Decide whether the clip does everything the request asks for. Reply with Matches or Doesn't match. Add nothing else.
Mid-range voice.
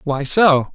Matches